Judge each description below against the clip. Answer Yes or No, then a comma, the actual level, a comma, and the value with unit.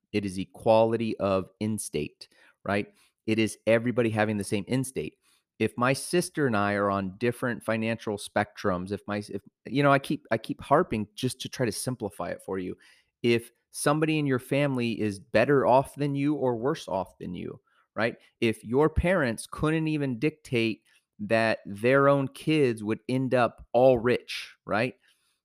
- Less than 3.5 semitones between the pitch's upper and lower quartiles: No, average, 4.1 semitones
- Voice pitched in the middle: No, low, 115 Hz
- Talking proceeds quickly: No, average, 170 wpm